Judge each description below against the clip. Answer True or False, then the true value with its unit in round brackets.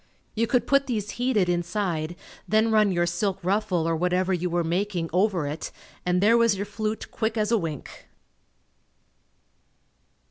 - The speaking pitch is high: True (195 Hz)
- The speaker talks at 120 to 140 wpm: False (155 wpm)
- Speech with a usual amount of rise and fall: True (3.8 semitones)